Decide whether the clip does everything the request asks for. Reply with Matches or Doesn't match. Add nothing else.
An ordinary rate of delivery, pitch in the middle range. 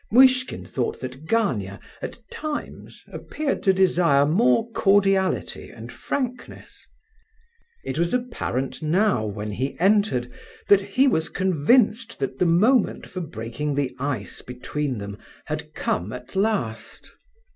Doesn't match